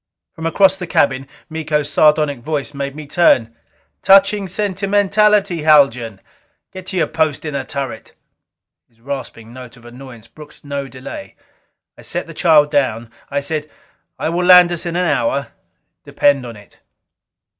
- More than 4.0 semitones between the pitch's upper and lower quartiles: Yes, average, 4.8 semitones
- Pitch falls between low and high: Yes, medium, 150 Hz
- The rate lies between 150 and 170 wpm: Yes, average, 155 wpm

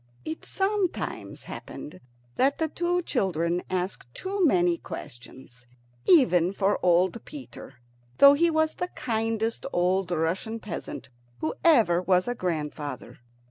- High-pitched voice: Yes, high, 195 Hz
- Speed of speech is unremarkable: No, slow, 125 wpm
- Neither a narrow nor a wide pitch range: No, wide, 8.9 semitones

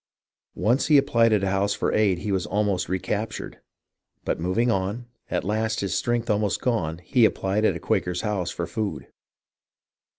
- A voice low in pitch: Yes, low, 105 Hz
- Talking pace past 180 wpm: No, average, 175 wpm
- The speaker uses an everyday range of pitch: Yes, average, 3.2 semitones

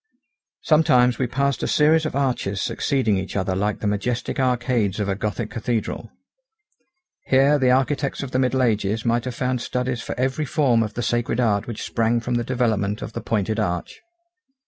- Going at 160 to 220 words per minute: Yes, average, 185 wpm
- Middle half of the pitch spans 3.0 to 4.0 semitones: Yes, average, 3.4 semitones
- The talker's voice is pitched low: Yes, low, 120 Hz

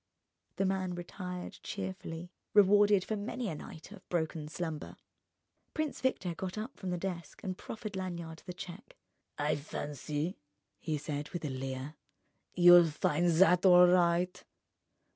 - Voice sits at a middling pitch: Yes, medium, 180 Hz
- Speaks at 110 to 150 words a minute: Yes, average, 140 wpm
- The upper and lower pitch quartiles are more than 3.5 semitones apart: No, average, 3.1 semitones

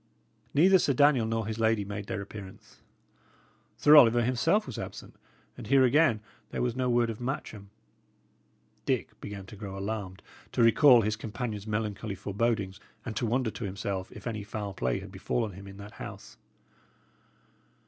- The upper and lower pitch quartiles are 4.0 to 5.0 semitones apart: No, average, 3.3 semitones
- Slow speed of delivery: No, average, 165 wpm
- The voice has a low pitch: Yes, low, 110 Hz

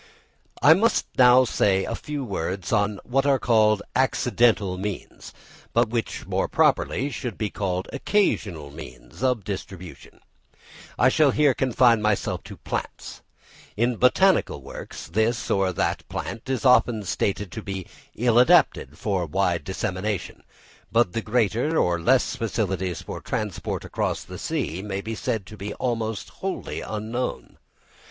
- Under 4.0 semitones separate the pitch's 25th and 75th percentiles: No, average, 4.4 semitones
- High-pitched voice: No, low, 110 Hz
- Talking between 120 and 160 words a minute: Yes, average, 145 wpm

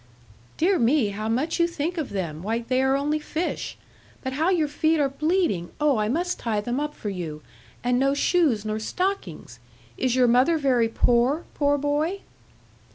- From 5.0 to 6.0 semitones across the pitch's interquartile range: Yes, wide, 5.6 semitones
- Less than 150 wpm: No, average, 180 wpm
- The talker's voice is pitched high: Yes, very high, 270 Hz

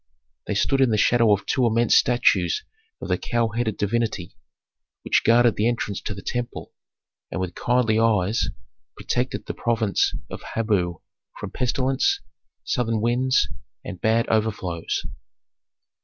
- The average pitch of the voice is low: Yes, low, 115 Hz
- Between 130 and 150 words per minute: Yes, average, 140 wpm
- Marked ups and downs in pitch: No, average, 2.7 semitones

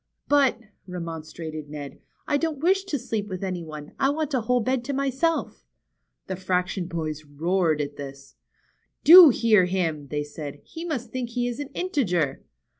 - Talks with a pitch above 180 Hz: Yes, high, 190 Hz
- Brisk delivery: No, average, 170 wpm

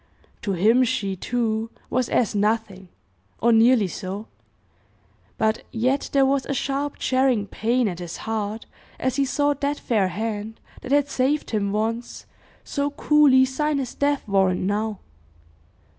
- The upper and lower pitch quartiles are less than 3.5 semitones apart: No, average, 4.5 semitones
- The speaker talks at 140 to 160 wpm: Yes, average, 145 wpm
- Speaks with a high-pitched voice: Yes, high, 230 Hz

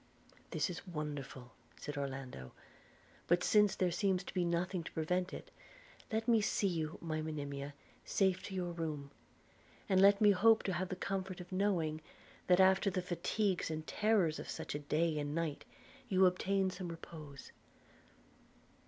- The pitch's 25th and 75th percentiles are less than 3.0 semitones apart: No, average, 3.6 semitones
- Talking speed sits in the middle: Yes, average, 160 wpm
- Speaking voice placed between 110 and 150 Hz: No, medium, 175 Hz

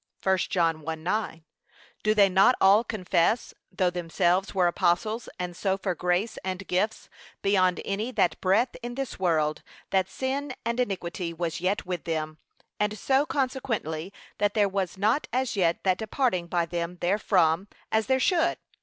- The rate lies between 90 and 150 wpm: No, average, 160 wpm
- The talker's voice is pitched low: No, high, 190 Hz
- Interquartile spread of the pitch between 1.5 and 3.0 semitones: No, average, 4.0 semitones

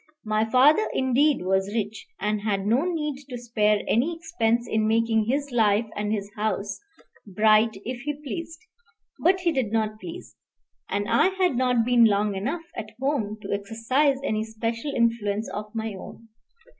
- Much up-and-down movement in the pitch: No, average, 4.2 semitones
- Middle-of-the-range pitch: No, high, 225 Hz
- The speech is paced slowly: No, average, 165 wpm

